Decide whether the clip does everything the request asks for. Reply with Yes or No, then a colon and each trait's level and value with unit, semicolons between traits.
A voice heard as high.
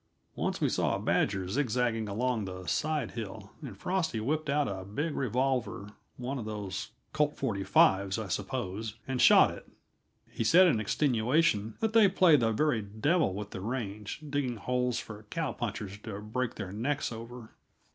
No: low, 115 Hz